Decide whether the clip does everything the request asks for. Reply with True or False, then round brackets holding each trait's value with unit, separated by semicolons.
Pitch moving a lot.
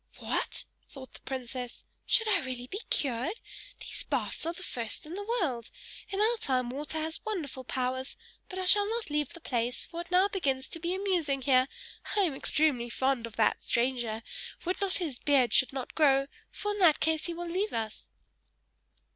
True (6.3 semitones)